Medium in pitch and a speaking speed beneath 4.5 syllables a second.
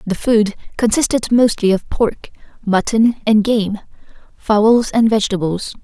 No: high, 215 Hz; 4.2 syllables/s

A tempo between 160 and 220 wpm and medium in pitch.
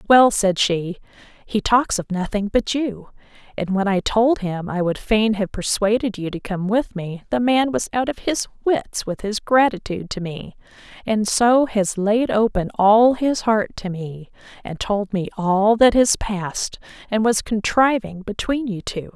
No: average, 185 wpm; high, 210 Hz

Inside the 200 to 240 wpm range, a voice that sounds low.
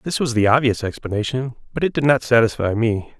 Yes: fast, 205 wpm; low, 120 Hz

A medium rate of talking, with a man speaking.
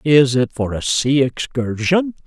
Yes: average, 160 wpm; male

